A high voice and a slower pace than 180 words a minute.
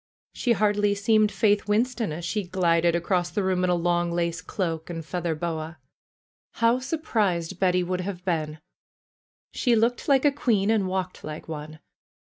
No: medium, 180 Hz; average, 165 wpm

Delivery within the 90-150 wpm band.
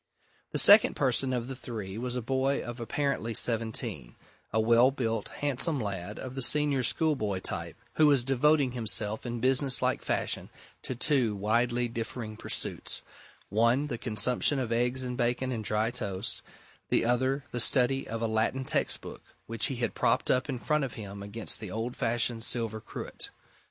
No: average, 170 wpm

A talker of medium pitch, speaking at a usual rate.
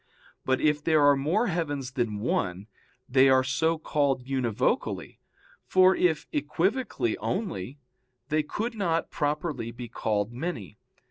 No: medium, 145 Hz; slow, 130 wpm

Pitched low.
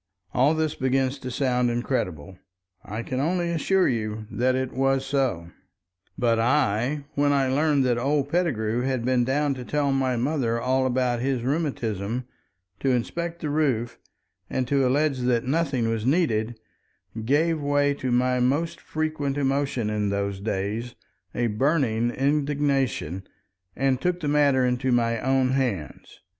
Yes: low, 130 Hz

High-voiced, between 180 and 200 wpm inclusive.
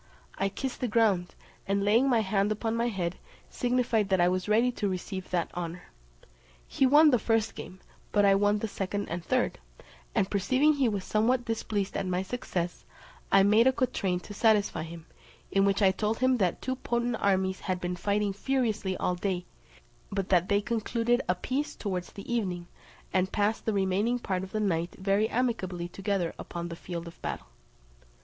Yes: high, 200 Hz; average, 185 wpm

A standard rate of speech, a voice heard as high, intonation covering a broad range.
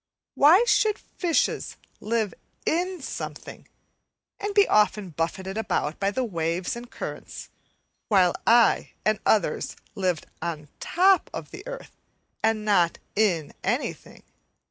No: slow, 120 wpm; high, 215 Hz; wide, 8.9 semitones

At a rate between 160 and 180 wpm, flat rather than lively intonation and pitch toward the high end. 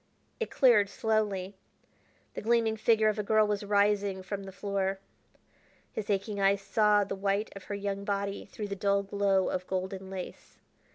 Yes: average, 170 wpm; narrow, 1.3 semitones; high, 200 Hz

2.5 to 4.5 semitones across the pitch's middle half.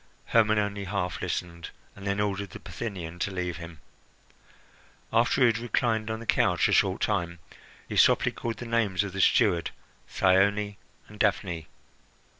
Yes: average, 3.4 semitones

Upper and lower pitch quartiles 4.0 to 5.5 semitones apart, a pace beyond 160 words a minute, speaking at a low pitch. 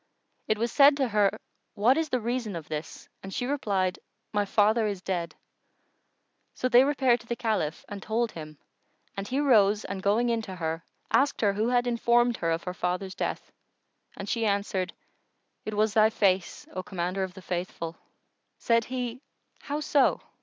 No: average, 4.4 semitones; average, 180 wpm; high, 210 Hz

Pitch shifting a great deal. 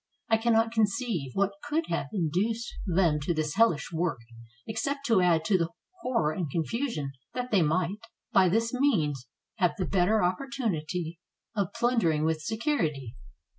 Yes: wide, 6.1 semitones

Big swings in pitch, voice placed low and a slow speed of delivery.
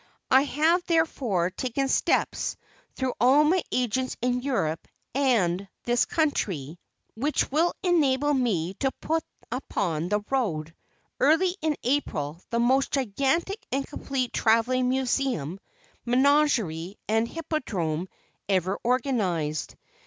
No: wide, 6.8 semitones; very high, 255 Hz; slow, 115 wpm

